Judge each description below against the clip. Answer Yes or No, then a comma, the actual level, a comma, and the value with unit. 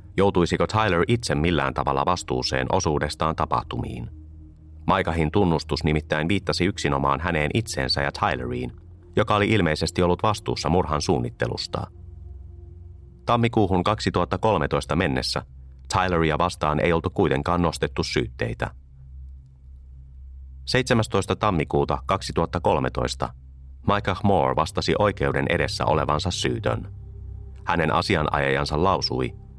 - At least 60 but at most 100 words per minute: Yes, slow, 95 wpm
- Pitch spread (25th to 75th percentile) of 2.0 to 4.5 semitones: No, wide, 5.5 semitones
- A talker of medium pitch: No, very low, 85 Hz